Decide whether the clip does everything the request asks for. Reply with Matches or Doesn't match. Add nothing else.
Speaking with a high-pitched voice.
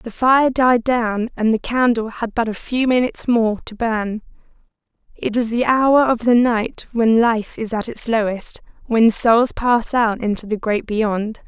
Matches